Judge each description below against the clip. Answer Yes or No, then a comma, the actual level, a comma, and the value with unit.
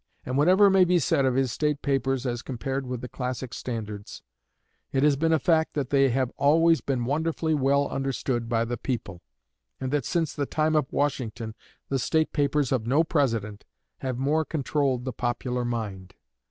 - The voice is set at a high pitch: No, low, 135 Hz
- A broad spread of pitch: No, average, 3.6 semitones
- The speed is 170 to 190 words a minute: Yes, average, 180 wpm